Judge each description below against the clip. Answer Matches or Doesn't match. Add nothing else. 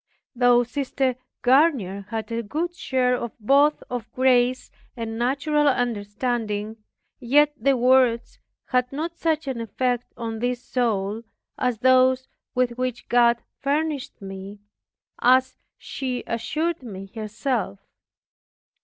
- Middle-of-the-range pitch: Doesn't match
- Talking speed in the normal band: Doesn't match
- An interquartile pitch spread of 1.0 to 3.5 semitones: Matches